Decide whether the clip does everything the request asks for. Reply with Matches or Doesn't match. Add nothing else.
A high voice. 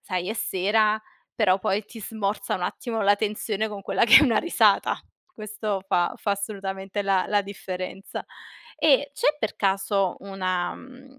Matches